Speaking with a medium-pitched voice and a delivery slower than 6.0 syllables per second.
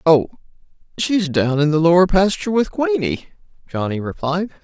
Yes: medium, 175 Hz; 5.1 syllables/s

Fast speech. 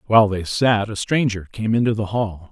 Yes: fast, 215 wpm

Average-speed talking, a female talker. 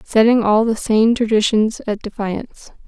Yes: average, 145 wpm; female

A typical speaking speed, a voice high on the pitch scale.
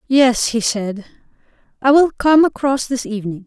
Yes: average, 155 wpm; high, 245 Hz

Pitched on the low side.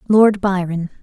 No: high, 190 Hz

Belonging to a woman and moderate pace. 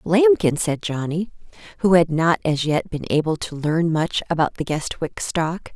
Yes: female; average, 175 wpm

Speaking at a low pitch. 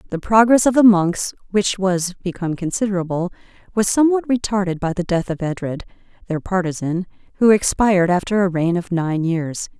No: high, 190 Hz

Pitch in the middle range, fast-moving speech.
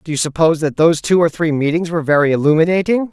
Yes: medium, 160 Hz; fast, 230 wpm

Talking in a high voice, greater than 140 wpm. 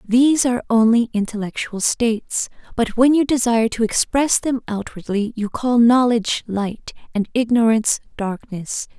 No: high, 230 Hz; slow, 135 wpm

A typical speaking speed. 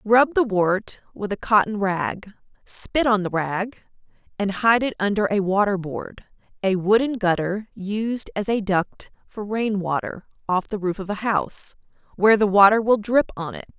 Yes: average, 180 wpm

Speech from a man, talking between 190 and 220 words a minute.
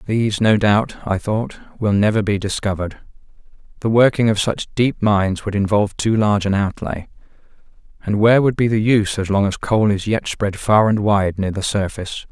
Yes: male; average, 195 wpm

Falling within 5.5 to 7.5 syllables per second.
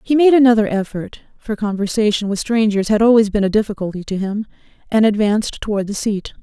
Yes: 6.0 syllables/s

